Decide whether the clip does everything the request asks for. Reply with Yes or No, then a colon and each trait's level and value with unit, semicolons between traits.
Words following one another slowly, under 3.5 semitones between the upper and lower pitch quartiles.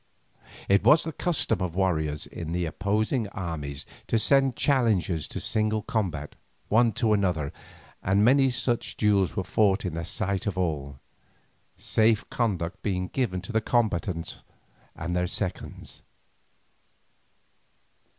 No: slow, 130 wpm; average, 4.3 semitones